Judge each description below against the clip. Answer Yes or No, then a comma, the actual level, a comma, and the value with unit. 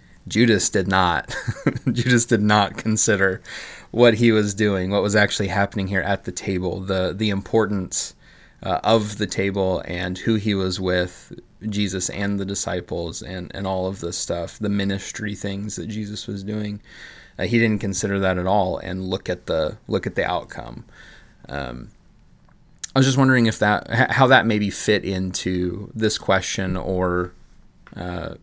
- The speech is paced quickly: No, average, 165 wpm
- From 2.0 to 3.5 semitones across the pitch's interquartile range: Yes, narrow, 2.6 semitones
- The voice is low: Yes, low, 100 Hz